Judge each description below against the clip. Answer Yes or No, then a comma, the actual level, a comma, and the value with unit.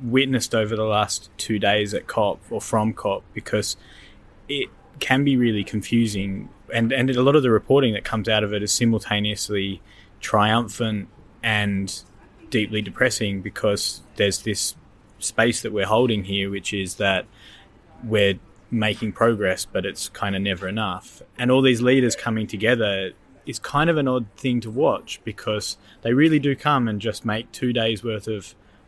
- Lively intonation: No, average, 2.7 semitones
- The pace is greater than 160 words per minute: Yes, average, 170 wpm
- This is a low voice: Yes, low, 110 Hz